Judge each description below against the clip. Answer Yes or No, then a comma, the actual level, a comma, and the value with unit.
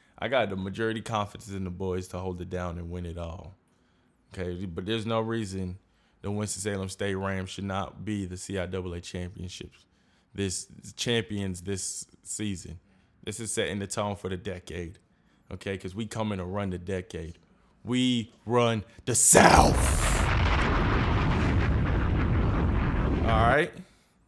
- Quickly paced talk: No, average, 145 wpm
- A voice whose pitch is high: No, very low, 95 Hz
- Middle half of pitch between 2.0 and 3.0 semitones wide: Yes, narrow, 2.5 semitones